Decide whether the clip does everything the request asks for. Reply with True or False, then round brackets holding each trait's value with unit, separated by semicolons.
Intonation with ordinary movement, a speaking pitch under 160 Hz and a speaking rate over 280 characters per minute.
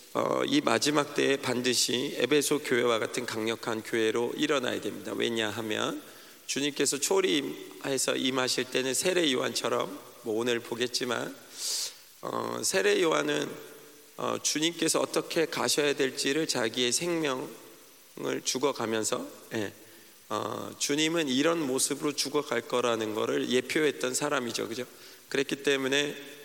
True (4.0 semitones; 140 Hz; 290 characters per minute)